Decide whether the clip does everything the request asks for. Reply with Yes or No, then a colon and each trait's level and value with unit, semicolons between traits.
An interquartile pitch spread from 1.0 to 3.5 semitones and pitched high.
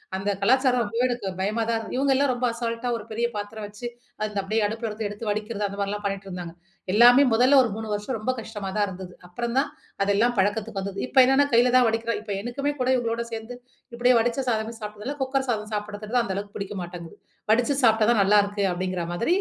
Yes: average, 2.9 semitones; high, 220 Hz